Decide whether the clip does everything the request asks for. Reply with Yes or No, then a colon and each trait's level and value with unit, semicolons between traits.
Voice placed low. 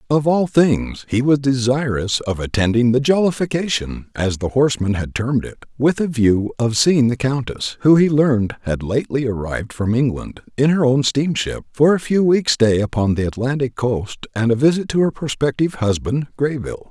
Yes: low, 130 Hz